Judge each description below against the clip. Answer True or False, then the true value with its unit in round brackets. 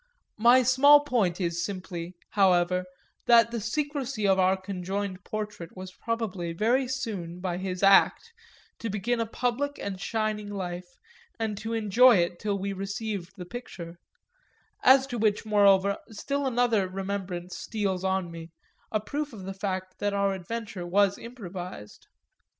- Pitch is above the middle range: True (200 Hz)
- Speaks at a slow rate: False (150 wpm)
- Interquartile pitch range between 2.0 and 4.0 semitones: True (3.7 semitones)